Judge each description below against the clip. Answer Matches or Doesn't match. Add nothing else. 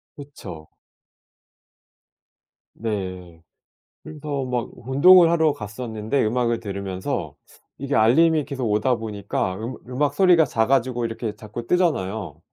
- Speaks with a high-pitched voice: Doesn't match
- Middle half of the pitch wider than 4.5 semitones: Matches